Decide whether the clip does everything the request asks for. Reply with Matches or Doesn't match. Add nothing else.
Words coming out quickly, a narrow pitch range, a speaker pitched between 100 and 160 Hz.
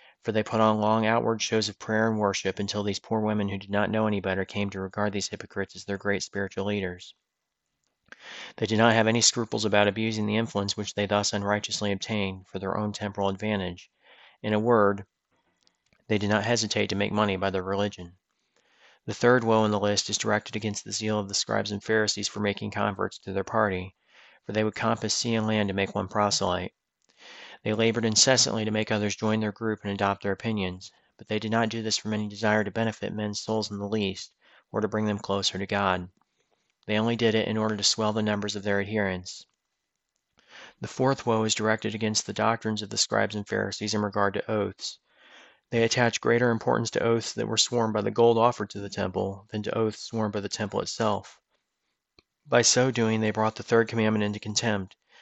Matches